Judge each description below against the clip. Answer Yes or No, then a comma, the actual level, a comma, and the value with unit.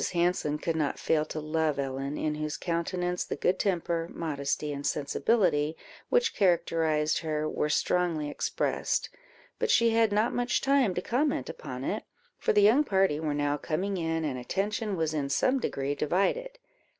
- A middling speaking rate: Yes, average, 165 wpm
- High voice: No, medium, 165 Hz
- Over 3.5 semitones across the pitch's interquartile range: Yes, average, 5.1 semitones